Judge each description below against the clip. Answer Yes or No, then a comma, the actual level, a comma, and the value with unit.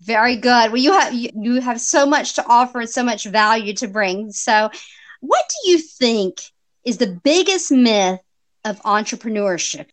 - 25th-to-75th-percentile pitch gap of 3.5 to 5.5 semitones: No, average, 2.7 semitones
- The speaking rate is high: No, average, 170 wpm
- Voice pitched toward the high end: Yes, high, 235 Hz